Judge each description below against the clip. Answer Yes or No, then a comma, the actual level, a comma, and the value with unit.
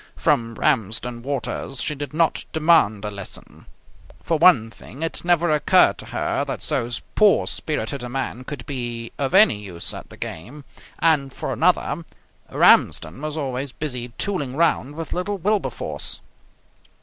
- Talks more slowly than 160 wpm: Yes, average, 150 wpm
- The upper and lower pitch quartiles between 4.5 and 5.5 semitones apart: Yes, average, 5.1 semitones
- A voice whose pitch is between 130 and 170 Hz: Yes, medium, 140 Hz